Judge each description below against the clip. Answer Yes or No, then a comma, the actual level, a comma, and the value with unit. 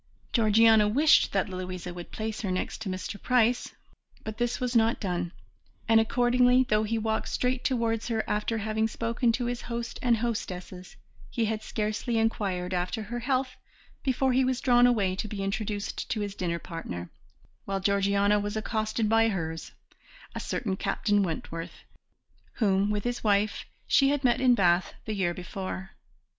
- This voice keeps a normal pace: Yes, average, 165 wpm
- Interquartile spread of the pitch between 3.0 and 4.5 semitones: Yes, average, 3.5 semitones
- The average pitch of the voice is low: No, high, 215 Hz